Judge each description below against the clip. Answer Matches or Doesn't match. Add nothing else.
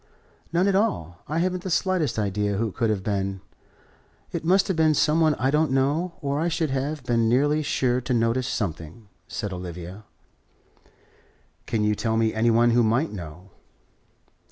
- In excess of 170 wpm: Matches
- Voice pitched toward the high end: Doesn't match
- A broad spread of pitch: Matches